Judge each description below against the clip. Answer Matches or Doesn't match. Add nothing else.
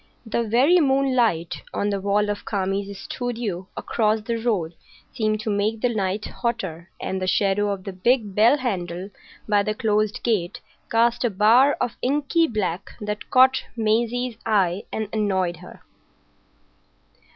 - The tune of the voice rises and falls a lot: Doesn't match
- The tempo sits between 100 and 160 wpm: Matches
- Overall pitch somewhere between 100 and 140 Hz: Doesn't match